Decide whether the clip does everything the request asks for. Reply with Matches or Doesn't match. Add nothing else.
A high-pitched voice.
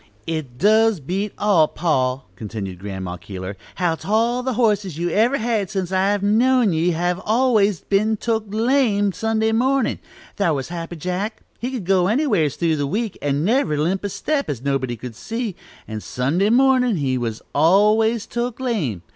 Matches